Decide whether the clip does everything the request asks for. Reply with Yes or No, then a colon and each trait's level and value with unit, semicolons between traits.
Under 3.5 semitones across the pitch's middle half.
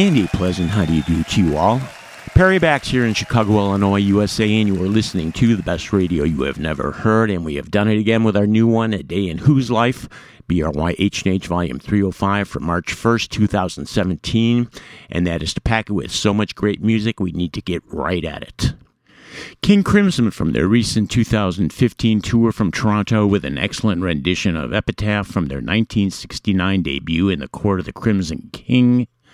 No: average, 4.0 semitones